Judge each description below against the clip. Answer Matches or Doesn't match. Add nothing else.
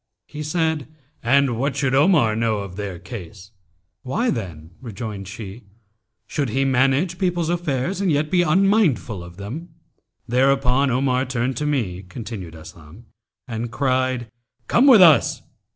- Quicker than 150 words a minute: Doesn't match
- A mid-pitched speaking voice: Doesn't match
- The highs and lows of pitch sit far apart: Matches